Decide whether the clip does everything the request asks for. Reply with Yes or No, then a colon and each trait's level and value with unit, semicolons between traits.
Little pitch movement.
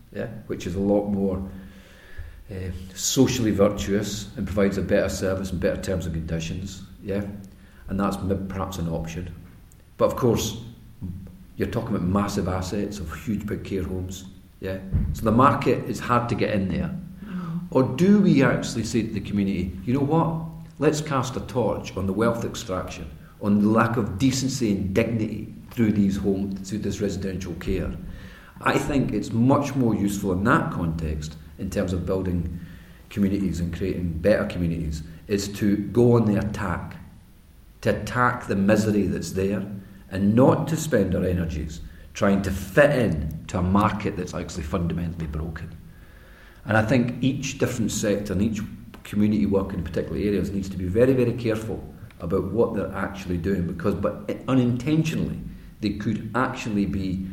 No: average, 3.4 semitones